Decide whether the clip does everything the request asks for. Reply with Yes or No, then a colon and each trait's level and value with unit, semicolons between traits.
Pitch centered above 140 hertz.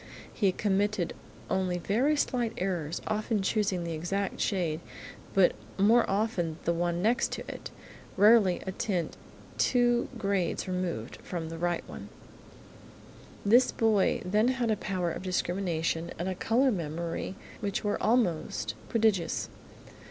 Yes: high, 190 Hz